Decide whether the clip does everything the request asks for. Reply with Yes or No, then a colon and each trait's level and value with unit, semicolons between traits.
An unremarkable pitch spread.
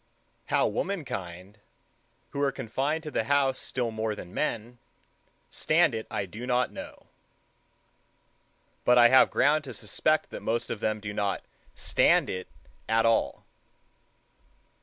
Yes: average, 4.2 semitones